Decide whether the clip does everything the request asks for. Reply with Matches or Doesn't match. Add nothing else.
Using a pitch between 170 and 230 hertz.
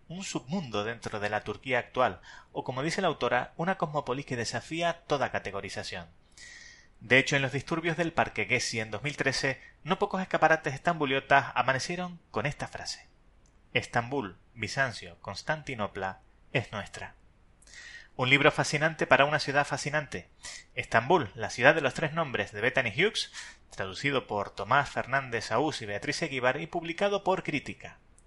Doesn't match